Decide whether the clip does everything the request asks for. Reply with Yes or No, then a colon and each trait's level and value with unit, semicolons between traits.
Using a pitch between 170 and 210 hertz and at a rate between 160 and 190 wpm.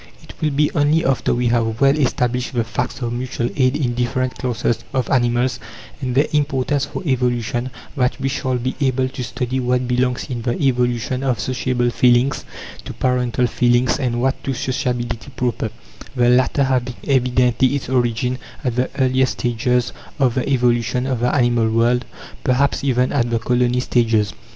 No: low, 125 Hz; average, 170 wpm